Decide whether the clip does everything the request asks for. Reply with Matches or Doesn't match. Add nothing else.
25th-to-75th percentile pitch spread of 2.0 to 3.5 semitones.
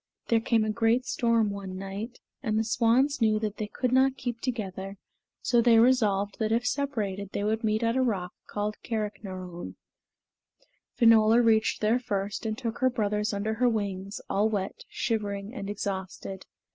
Matches